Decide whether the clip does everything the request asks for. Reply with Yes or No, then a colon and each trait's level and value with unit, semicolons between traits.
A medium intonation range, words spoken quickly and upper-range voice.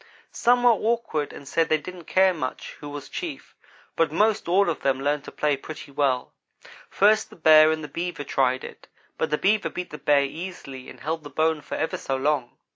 No: average, 4.3 semitones; fast, 210 wpm; medium, 155 Hz